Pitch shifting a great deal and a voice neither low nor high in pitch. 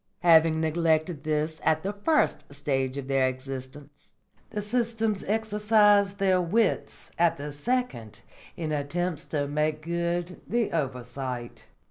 Yes: wide, 6.0 semitones; medium, 160 Hz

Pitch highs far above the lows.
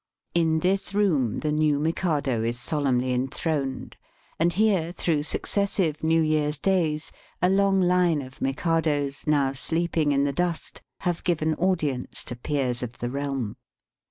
No: average, 3.9 semitones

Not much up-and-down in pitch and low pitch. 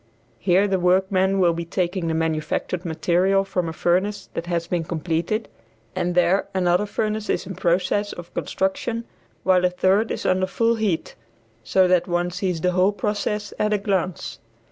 No: narrow, 2.3 semitones; medium, 185 Hz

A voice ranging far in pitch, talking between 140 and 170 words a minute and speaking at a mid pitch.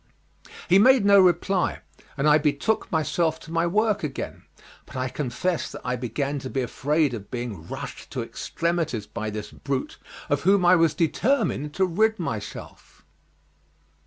Yes: wide, 6.0 semitones; average, 160 wpm; medium, 155 Hz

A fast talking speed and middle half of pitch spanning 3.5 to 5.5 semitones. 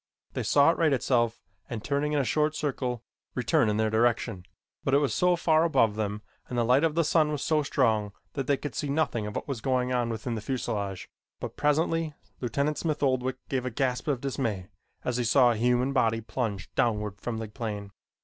Yes: fast, 210 wpm; average, 4.3 semitones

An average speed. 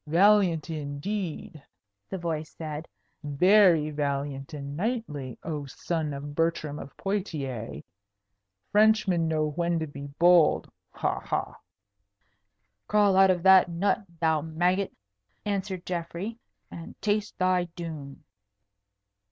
No: slow, 110 wpm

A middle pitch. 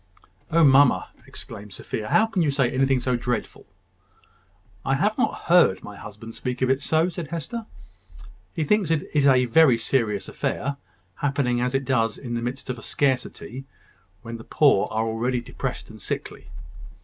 No: low, 130 Hz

